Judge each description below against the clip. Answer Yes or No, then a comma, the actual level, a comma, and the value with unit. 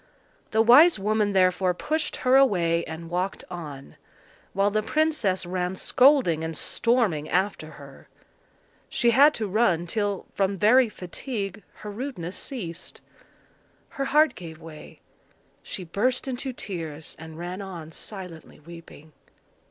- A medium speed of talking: No, slow, 130 wpm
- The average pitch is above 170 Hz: Yes, high, 190 Hz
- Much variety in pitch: Yes, wide, 6.0 semitones